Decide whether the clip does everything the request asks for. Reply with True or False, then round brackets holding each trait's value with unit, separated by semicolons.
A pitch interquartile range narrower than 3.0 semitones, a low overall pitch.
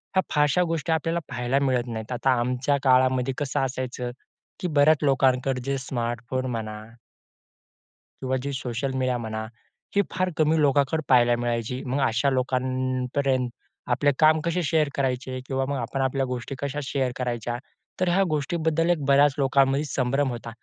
True (2.4 semitones; 130 Hz)